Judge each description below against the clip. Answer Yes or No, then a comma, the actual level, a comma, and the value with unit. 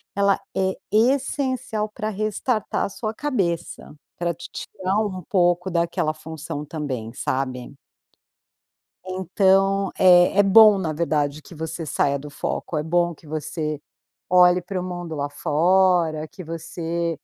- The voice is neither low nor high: Yes, medium, 175 Hz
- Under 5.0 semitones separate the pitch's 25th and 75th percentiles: Yes, average, 3.8 semitones